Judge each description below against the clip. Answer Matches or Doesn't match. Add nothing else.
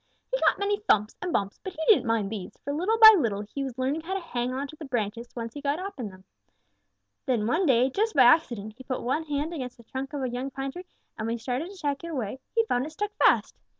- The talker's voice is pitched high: Matches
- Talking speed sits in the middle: Doesn't match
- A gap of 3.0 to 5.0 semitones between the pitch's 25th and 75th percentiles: Doesn't match